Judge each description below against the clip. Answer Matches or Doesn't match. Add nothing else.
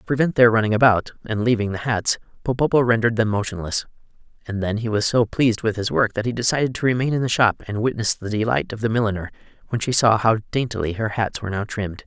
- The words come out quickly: Matches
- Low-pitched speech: Matches